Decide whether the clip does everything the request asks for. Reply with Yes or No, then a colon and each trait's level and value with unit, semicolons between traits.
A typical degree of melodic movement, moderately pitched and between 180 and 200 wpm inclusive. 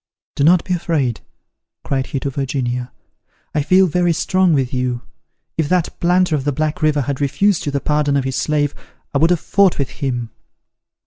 Yes: average, 4.2 semitones; medium, 145 Hz; average, 190 wpm